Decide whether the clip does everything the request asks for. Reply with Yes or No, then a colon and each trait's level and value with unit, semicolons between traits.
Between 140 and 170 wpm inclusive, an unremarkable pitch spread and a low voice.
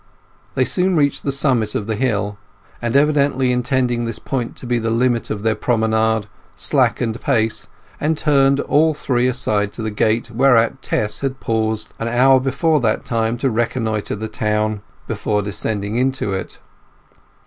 Yes: average, 160 wpm; average, 3.3 semitones; low, 120 Hz